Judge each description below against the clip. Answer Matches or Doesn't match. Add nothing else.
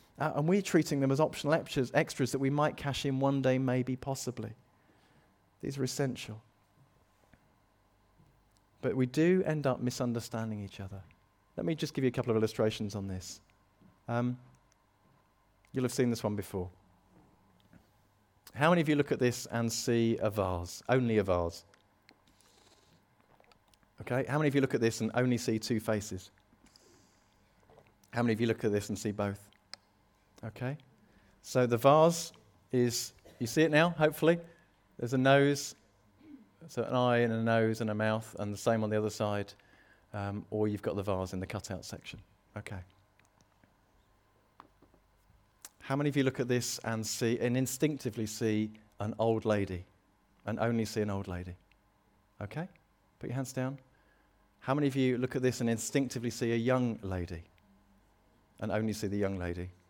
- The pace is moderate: Matches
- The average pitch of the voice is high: Doesn't match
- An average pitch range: Matches